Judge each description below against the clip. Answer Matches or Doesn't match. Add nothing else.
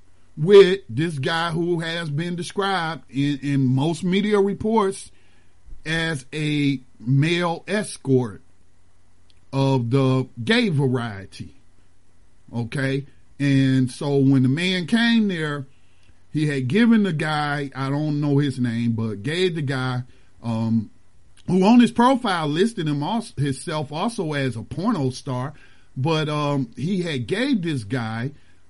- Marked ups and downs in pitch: Matches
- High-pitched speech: Doesn't match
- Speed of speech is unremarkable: Doesn't match